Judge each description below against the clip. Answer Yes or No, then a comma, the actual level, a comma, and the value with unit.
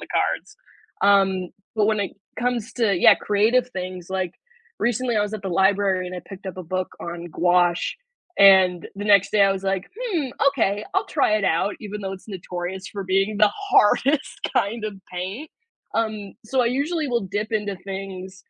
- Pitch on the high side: Yes, high, 200 Hz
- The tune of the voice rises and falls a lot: No, narrow, 2.5 semitones